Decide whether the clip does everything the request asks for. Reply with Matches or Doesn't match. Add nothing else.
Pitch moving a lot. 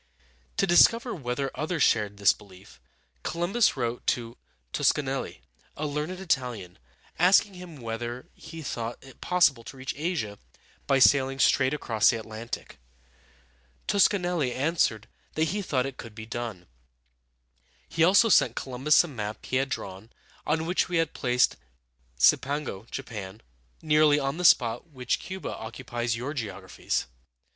Matches